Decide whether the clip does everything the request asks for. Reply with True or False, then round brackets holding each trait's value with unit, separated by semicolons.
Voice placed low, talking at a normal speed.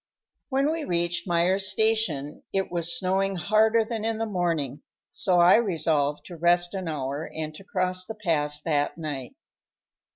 False (175 Hz; 160 wpm)